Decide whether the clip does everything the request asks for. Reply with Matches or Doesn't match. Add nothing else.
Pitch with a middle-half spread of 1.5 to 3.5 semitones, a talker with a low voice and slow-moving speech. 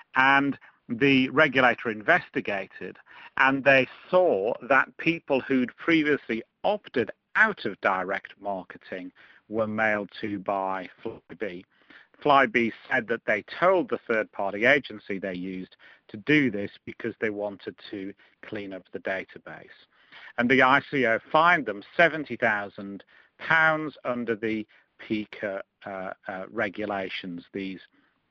Doesn't match